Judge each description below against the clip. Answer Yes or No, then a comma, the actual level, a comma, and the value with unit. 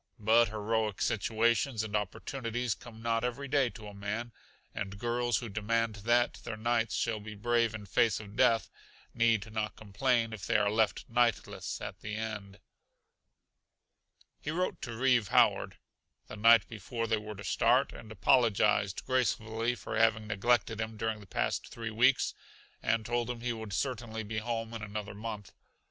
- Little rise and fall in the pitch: Yes, narrow, 1.9 semitones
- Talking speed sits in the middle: Yes, average, 165 wpm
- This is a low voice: Yes, low, 110 Hz